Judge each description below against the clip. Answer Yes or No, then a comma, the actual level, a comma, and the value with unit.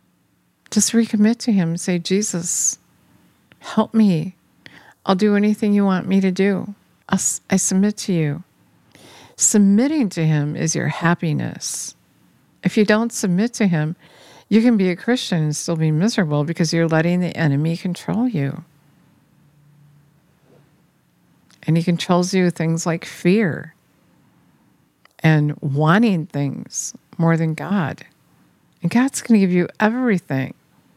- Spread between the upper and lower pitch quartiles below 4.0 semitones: No, average, 4.4 semitones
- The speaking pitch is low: No, medium, 175 Hz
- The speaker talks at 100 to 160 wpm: Yes, average, 140 wpm